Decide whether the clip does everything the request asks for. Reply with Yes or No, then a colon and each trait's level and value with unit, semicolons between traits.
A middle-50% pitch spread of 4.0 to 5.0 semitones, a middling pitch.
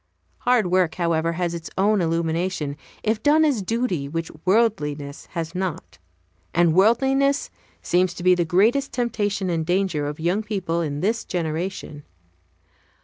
Yes: average, 4.5 semitones; medium, 180 Hz